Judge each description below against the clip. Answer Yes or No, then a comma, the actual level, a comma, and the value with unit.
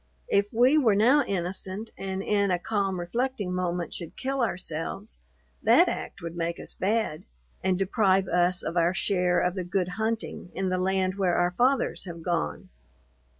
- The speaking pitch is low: No, high, 190 Hz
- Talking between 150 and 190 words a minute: Yes, average, 170 wpm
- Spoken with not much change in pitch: No, average, 3.1 semitones